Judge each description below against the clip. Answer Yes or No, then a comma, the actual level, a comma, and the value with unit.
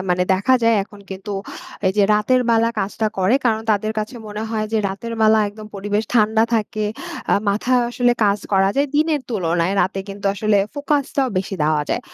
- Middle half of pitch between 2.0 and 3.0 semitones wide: Yes, average, 2.7 semitones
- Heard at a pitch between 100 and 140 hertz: No, high, 215 Hz